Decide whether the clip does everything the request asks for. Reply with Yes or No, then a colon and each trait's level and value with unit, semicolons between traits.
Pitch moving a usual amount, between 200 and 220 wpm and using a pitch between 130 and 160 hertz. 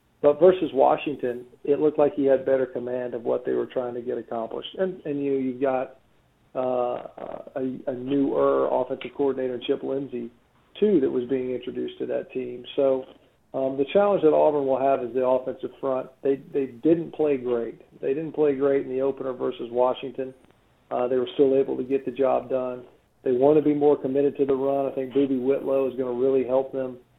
No: narrow, 1.8 semitones; fast, 205 wpm; low, 135 Hz